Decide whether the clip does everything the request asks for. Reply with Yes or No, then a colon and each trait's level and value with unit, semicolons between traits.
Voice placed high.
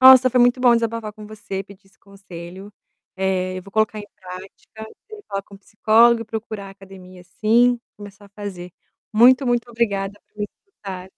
Yes: high, 205 Hz